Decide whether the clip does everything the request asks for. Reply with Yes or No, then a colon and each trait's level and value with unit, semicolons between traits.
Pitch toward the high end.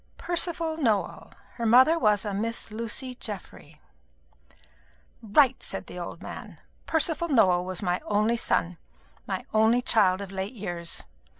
Yes: high, 220 Hz